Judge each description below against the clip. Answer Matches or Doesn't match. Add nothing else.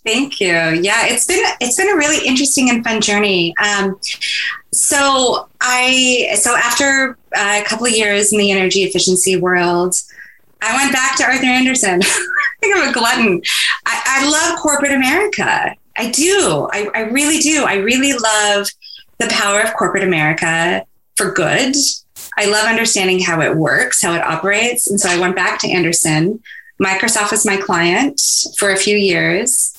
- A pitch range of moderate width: Doesn't match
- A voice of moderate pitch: Doesn't match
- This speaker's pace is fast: Doesn't match